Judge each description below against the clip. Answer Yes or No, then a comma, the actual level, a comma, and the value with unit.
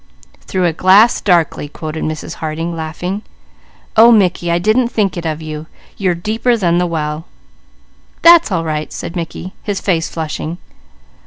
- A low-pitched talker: No, medium, 175 Hz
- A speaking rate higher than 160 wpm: No, average, 155 wpm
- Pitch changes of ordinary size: Yes, average, 3.9 semitones